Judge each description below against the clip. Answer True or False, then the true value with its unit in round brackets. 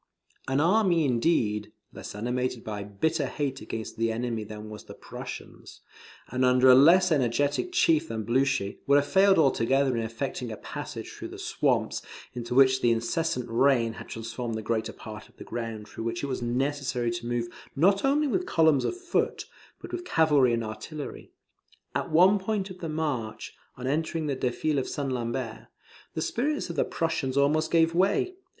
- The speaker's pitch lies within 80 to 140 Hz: True (135 Hz)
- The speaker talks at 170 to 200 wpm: True (180 wpm)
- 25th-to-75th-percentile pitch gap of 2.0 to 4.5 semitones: False (5.6 semitones)